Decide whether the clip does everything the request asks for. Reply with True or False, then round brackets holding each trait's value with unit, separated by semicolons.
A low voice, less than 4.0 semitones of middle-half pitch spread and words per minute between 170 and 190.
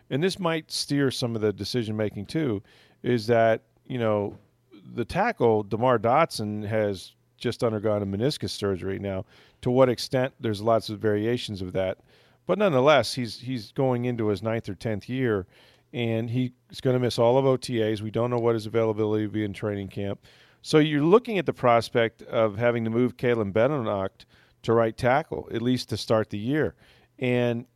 True (115 Hz; 2.8 semitones; 185 wpm)